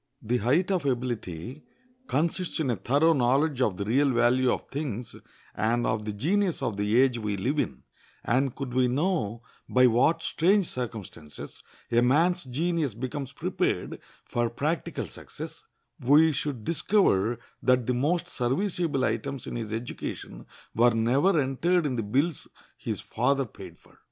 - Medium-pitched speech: No, low, 130 Hz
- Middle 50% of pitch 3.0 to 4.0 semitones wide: No, average, 4.6 semitones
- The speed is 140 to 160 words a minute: Yes, average, 155 wpm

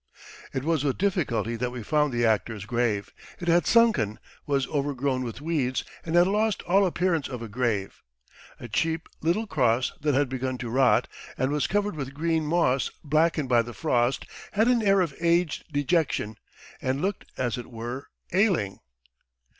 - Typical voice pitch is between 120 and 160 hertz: Yes, medium, 140 Hz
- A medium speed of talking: Yes, average, 170 wpm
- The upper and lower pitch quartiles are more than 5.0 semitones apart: Yes, wide, 5.6 semitones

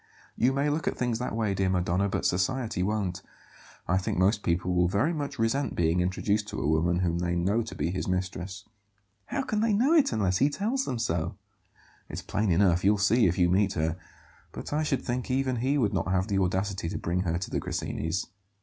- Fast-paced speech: Yes, fast, 220 wpm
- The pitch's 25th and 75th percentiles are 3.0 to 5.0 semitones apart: No, wide, 5.5 semitones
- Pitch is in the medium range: No, very low, 95 Hz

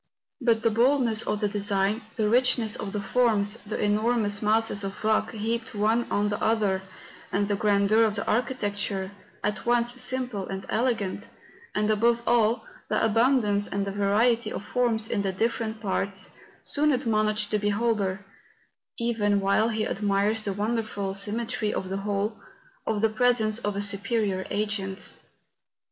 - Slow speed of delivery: No, average, 155 wpm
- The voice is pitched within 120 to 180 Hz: No, high, 215 Hz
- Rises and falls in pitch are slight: Yes, narrow, 2.3 semitones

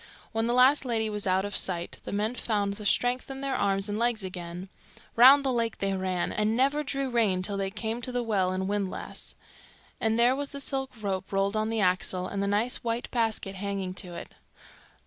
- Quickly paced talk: Yes, fast, 215 wpm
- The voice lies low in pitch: No, high, 215 Hz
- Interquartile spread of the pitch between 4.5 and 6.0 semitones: No, average, 3.8 semitones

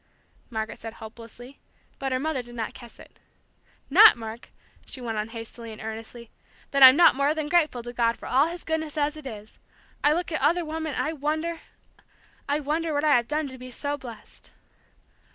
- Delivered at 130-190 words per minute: No, average, 200 wpm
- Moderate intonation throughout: Yes, average, 4.8 semitones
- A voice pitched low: No, very high, 270 Hz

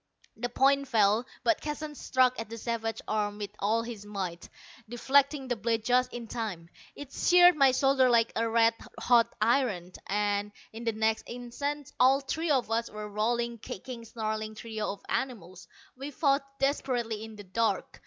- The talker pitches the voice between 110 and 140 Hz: No, high, 230 Hz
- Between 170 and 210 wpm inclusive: Yes, average, 175 wpm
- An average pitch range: Yes, average, 3.5 semitones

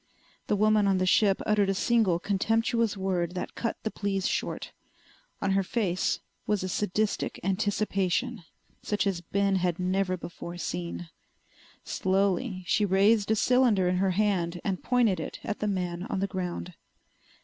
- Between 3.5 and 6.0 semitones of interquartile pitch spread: No, narrow, 2.5 semitones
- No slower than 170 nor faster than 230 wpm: No, average, 160 wpm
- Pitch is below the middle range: No, high, 195 Hz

